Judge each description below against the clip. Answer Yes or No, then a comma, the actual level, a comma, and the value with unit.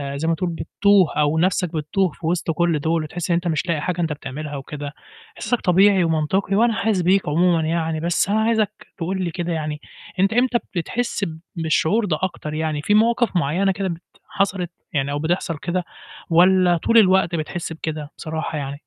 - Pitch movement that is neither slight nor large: Yes, average, 3.3 semitones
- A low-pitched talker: No, medium, 170 Hz